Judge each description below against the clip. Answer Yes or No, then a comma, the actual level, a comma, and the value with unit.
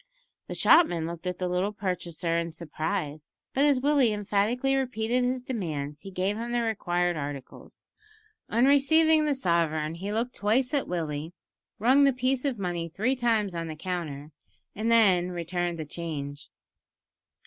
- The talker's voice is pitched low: No, high, 190 Hz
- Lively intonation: Yes, wide, 6.6 semitones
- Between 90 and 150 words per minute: No, average, 160 wpm